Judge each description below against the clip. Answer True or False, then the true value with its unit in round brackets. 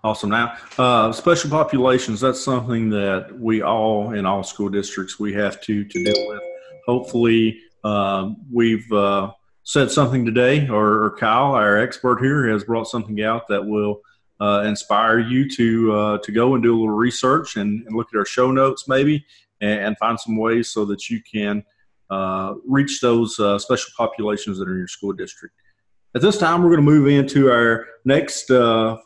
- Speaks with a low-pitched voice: True (115 Hz)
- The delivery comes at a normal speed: True (185 wpm)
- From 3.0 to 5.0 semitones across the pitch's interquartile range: True (3.7 semitones)